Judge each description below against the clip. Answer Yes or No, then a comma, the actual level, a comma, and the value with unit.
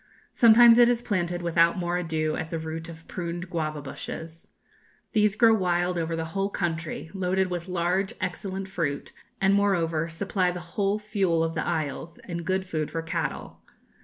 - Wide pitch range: No, average, 2.8 semitones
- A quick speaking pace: No, average, 170 wpm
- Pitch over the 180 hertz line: No, medium, 175 Hz